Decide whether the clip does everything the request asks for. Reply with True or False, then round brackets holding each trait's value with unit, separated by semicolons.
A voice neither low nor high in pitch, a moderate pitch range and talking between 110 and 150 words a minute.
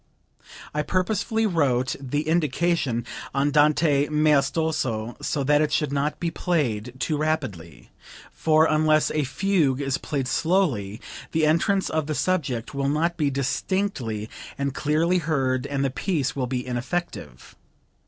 True (150 Hz; 3.6 semitones; 135 wpm)